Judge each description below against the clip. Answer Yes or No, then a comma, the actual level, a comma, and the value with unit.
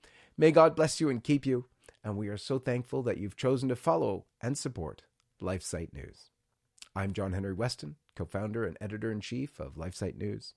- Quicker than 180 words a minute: No, average, 175 wpm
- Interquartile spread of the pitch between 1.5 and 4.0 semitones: No, wide, 5.5 semitones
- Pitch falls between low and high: No, low, 105 Hz